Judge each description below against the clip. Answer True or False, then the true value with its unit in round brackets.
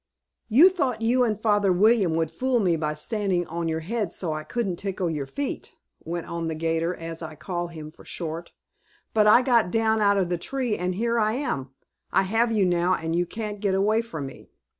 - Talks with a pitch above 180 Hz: True (190 Hz)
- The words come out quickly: True (215 wpm)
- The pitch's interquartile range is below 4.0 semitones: False (5.2 semitones)